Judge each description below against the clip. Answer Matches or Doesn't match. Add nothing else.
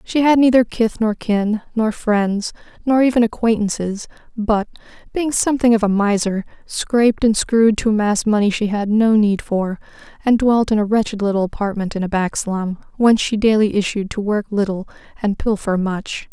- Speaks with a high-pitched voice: Matches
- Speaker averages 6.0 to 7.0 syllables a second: Doesn't match